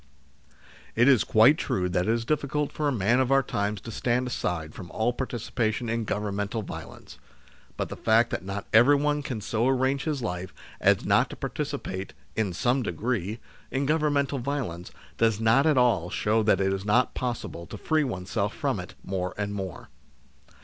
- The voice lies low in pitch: Yes, low, 115 Hz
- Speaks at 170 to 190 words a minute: Yes, average, 180 wpm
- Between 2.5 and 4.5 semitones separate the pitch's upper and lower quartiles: No, average, 5.0 semitones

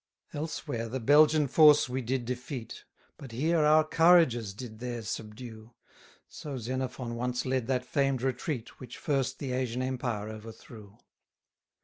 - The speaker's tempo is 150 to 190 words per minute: No, average, 140 wpm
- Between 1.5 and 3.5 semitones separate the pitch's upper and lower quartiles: Yes, average, 3.1 semitones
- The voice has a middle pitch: No, low, 125 Hz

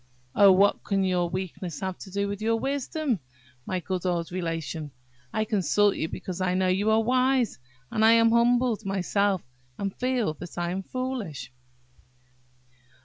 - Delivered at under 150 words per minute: No, average, 160 wpm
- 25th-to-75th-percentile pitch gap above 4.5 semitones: No, average, 4.0 semitones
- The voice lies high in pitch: Yes, high, 195 Hz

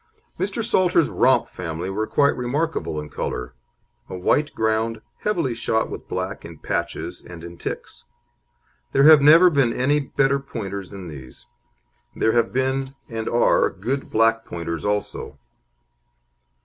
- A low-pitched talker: Yes, low, 115 Hz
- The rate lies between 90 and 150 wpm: Yes, average, 140 wpm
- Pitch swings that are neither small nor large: No, wide, 6.3 semitones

